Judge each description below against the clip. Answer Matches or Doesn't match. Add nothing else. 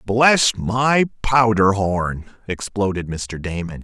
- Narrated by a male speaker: Matches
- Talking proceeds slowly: Matches